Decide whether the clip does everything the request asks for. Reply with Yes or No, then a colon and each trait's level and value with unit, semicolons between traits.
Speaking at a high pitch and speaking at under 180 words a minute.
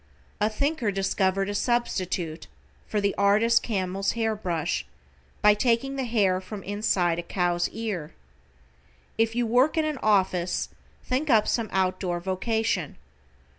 Yes: high, 205 Hz; average, 140 wpm